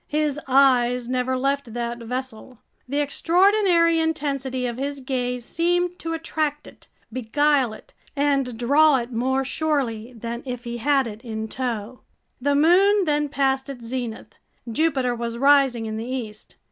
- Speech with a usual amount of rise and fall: Yes, average, 3.6 semitones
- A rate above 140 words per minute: Yes, average, 150 wpm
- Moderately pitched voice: No, very high, 265 Hz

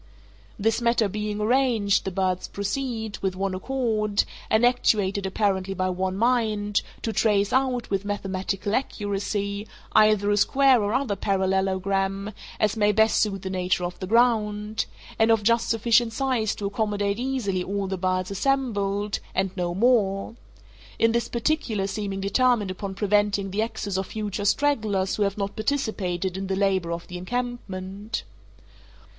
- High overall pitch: Yes, high, 205 Hz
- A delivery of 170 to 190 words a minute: No, average, 150 wpm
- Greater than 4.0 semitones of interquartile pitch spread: No, average, 2.7 semitones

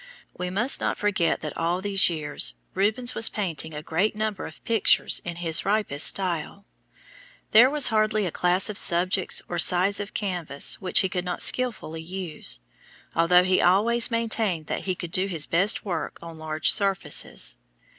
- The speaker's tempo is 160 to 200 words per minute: Yes, average, 170 wpm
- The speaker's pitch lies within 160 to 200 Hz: Yes, medium, 185 Hz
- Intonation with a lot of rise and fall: No, average, 3.7 semitones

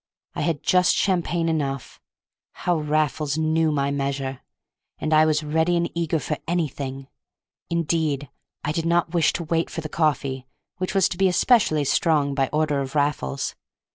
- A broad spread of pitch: No, average, 2.9 semitones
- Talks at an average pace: Yes, average, 160 wpm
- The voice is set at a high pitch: No, medium, 155 Hz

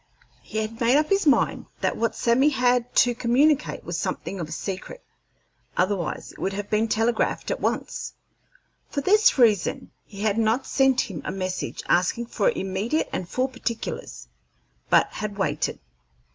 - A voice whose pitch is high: Yes, high, 230 Hz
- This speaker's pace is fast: No, average, 160 wpm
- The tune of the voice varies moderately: Yes, average, 4.8 semitones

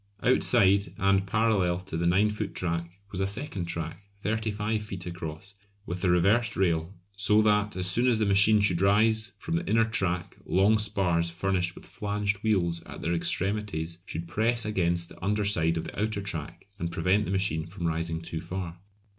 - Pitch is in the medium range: No, very low, 95 Hz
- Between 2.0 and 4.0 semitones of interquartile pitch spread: Yes, average, 3.5 semitones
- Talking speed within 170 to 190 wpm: Yes, average, 185 wpm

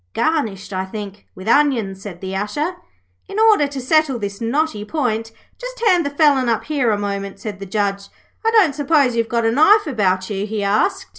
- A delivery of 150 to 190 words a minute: No, average, 200 wpm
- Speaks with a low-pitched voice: No, high, 230 Hz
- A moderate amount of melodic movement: No, wide, 6.9 semitones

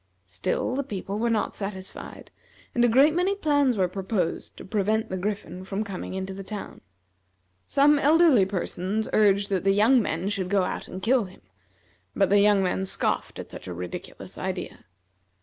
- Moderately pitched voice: No, high, 200 Hz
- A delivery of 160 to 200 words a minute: Yes, average, 180 wpm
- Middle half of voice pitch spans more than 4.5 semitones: No, average, 3.9 semitones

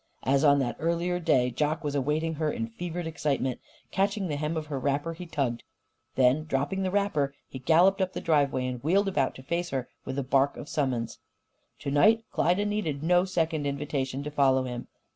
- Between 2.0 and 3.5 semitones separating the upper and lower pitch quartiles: No, average, 4.0 semitones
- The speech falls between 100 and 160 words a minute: No, average, 200 wpm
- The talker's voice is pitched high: No, medium, 150 Hz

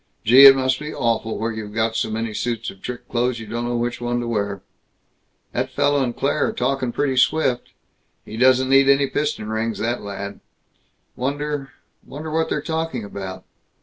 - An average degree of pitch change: Yes, average, 3.5 semitones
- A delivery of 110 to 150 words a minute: No, average, 185 wpm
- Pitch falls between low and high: No, low, 120 Hz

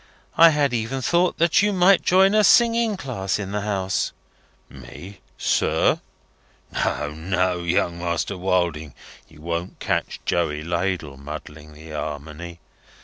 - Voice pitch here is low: Yes, very low, 90 Hz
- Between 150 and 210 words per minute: No, slow, 135 wpm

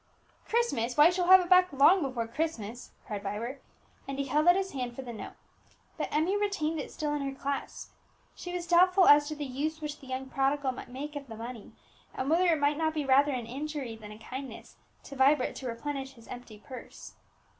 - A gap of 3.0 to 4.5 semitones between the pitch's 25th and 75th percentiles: Yes, average, 3.8 semitones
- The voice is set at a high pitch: Yes, very high, 280 Hz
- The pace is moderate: No, fast, 220 wpm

